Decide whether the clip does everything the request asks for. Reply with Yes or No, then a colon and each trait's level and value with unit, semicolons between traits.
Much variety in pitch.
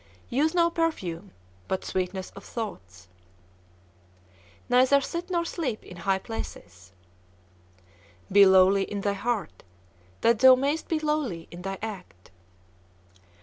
Yes: wide, 7.2 semitones